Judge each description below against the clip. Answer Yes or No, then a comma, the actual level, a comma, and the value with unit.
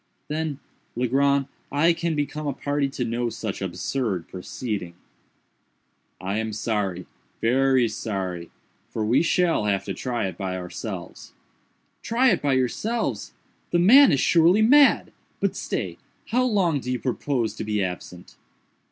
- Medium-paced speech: No, slow, 130 wpm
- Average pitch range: No, wide, 7.1 semitones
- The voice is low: Yes, low, 125 Hz